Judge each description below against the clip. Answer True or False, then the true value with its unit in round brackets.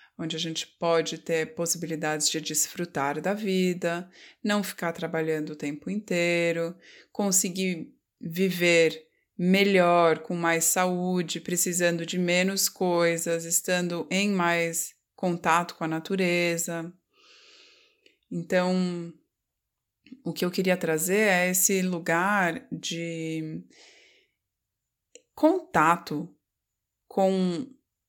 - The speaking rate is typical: False (95 wpm)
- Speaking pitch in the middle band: True (175 Hz)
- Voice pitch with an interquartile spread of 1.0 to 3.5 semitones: True (2.5 semitones)